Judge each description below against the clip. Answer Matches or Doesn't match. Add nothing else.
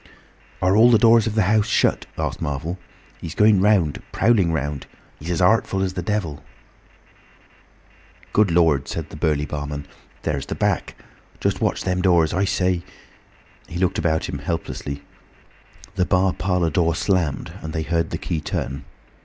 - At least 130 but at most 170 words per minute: Matches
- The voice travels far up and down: Doesn't match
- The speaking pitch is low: Matches